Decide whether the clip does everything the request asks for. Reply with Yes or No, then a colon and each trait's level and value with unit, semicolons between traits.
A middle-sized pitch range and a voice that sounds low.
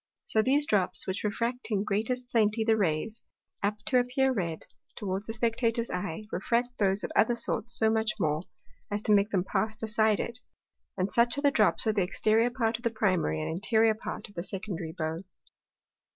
No: average, 3.1 semitones; high, 220 Hz